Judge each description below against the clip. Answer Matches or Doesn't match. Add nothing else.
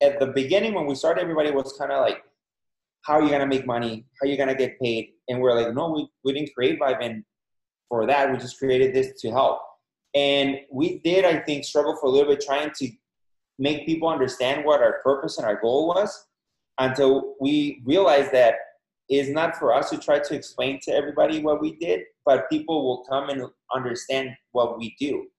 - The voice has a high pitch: Doesn't match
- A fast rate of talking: Matches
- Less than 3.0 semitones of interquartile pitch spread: Matches